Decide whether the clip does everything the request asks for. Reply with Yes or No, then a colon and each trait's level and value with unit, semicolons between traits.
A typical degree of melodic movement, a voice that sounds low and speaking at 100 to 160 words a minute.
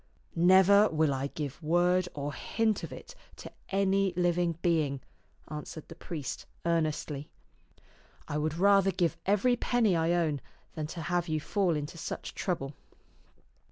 No: average, 3.7 semitones; medium, 170 Hz; average, 155 wpm